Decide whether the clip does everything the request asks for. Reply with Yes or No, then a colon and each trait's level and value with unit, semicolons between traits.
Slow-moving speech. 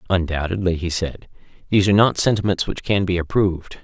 No: average, 170 wpm